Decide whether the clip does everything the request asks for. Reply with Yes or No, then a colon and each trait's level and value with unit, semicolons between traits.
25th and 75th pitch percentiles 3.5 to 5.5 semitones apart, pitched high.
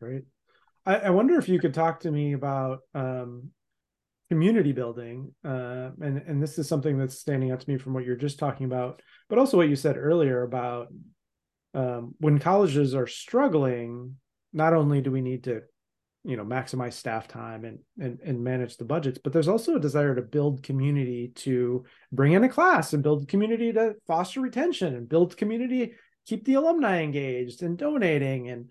No: average, 5.2 semitones; medium, 140 Hz